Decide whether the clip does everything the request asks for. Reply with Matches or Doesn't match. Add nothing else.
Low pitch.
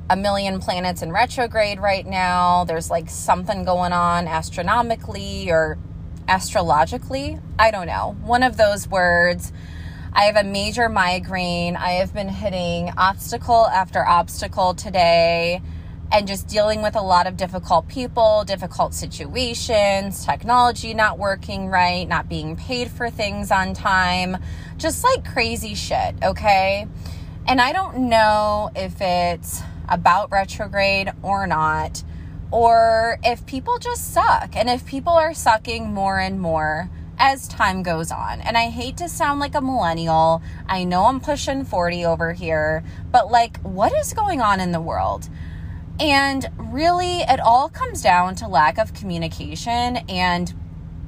Doesn't match